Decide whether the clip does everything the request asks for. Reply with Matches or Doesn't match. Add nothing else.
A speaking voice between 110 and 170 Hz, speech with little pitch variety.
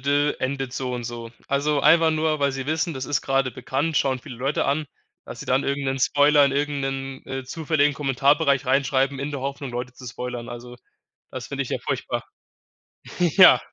Matches